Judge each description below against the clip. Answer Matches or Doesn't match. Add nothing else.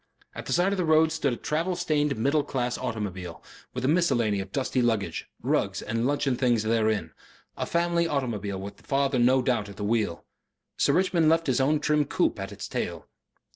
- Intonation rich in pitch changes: Matches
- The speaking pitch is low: Matches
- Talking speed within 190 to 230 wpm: Matches